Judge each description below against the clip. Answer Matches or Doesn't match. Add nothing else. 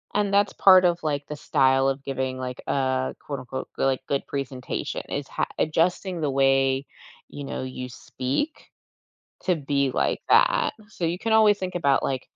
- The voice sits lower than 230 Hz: Matches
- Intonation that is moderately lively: Matches